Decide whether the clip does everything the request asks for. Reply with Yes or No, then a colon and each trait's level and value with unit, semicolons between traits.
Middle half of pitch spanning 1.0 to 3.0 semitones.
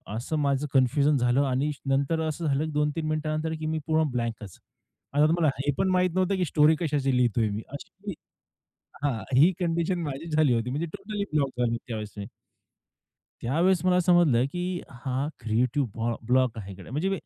No: average, 4.8 semitones